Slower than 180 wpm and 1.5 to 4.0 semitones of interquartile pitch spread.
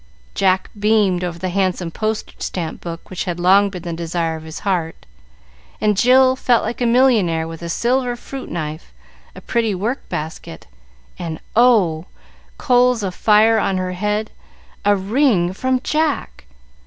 No: average, 155 wpm; average, 5.3 semitones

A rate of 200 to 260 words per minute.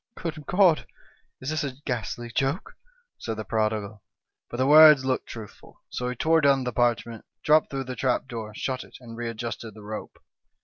Yes: fast, 205 wpm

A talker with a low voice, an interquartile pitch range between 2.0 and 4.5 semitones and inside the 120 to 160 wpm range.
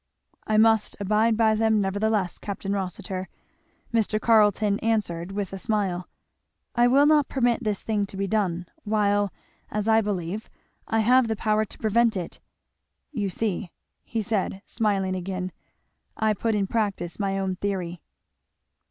No: high, 210 Hz; narrow, 2.4 semitones; average, 150 wpm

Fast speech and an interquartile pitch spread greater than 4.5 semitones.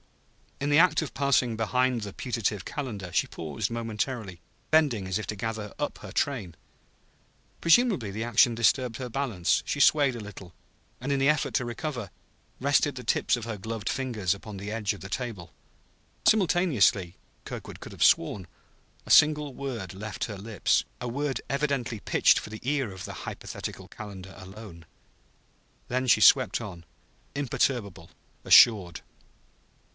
No: average, 155 wpm; average, 5.2 semitones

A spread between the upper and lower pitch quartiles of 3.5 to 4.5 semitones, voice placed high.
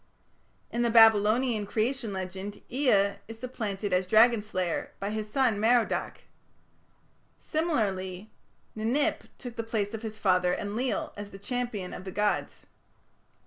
No: average, 3.0 semitones; high, 215 Hz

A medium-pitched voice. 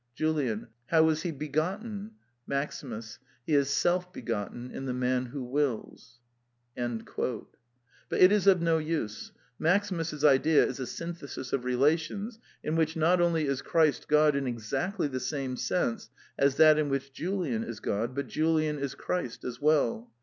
Yes: medium, 145 Hz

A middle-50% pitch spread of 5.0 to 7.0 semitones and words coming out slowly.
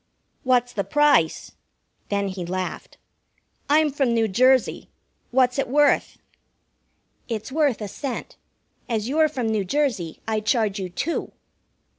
Yes: average, 5.3 semitones; slow, 130 wpm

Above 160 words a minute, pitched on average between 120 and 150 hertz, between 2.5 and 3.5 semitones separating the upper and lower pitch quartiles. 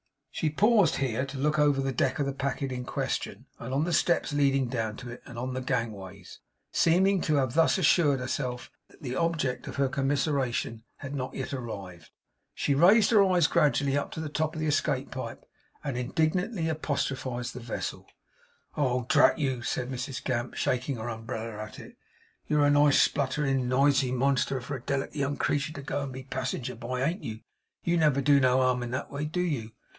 Yes: average, 200 wpm; low, 135 Hz; average, 2.9 semitones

